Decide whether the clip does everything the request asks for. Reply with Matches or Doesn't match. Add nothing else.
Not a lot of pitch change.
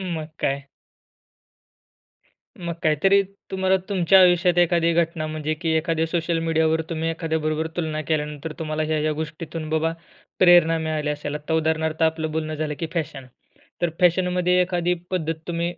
Matches